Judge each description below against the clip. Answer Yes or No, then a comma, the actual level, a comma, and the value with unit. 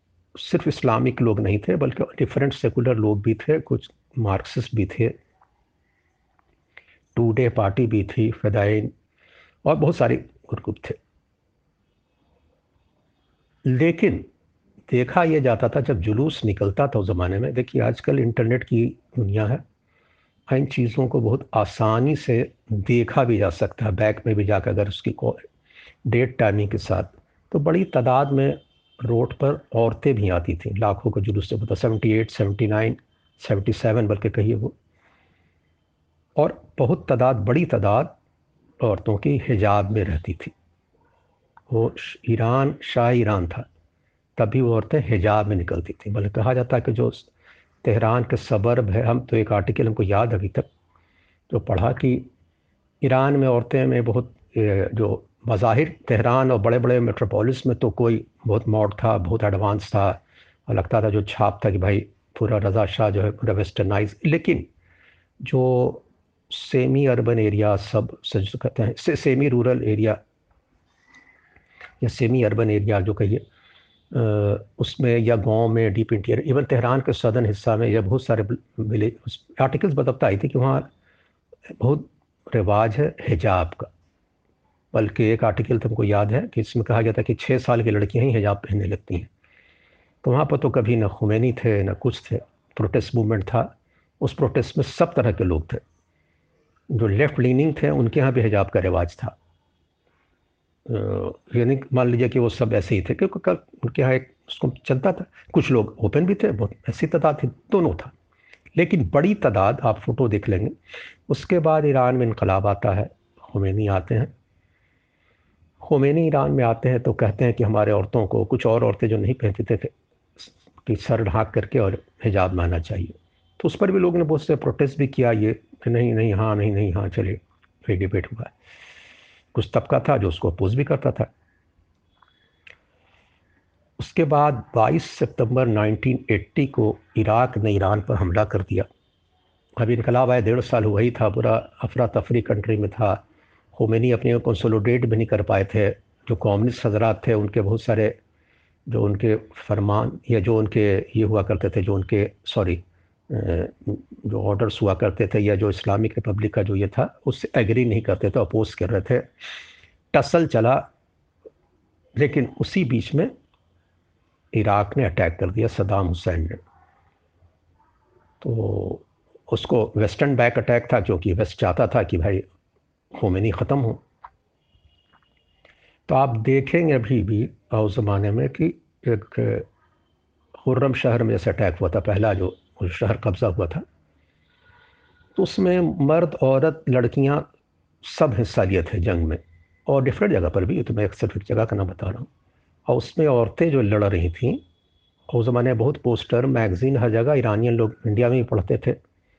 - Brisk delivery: No, average, 165 wpm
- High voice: No, low, 110 Hz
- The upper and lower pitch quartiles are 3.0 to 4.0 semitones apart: Yes, average, 3.6 semitones